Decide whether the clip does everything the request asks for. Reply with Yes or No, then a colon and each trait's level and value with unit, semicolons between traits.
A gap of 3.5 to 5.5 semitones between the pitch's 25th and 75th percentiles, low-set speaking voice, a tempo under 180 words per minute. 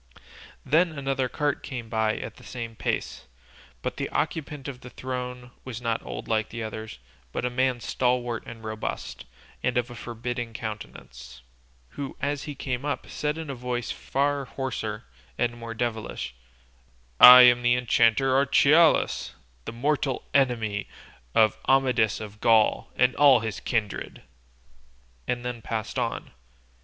No: average, 2.8 semitones; low, 125 Hz; average, 150 wpm